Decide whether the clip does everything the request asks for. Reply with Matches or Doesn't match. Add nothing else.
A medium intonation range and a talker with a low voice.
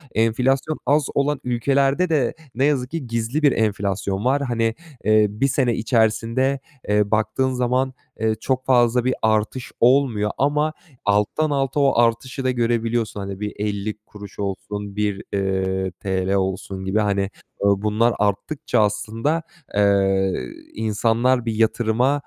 Matches